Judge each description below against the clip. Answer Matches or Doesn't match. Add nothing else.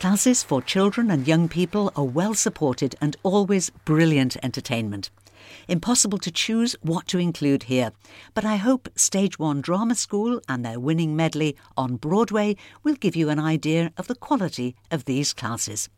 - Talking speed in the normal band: Matches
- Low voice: Doesn't match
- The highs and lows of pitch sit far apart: Matches